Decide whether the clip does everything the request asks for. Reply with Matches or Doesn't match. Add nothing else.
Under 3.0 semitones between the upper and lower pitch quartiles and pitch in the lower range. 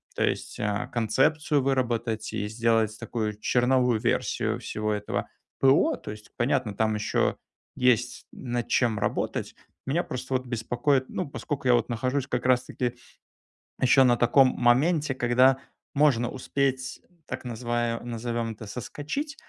Matches